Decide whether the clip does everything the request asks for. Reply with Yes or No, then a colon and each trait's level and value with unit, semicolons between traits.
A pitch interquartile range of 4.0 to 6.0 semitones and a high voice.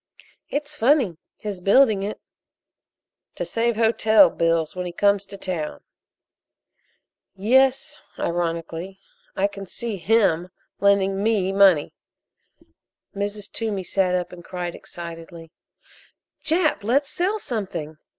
Yes: average, 4.4 semitones; high, 195 Hz